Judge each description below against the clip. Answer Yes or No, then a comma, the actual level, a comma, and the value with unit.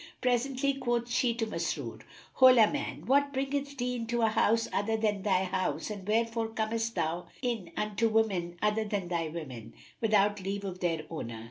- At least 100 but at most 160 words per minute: No, average, 170 wpm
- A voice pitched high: Yes, high, 220 Hz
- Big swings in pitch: No, average, 4.1 semitones